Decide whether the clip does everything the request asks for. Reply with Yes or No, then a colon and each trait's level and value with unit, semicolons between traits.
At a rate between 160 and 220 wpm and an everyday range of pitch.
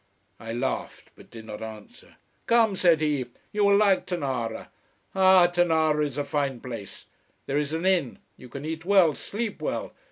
No: average, 170 wpm; wide, 6.3 semitones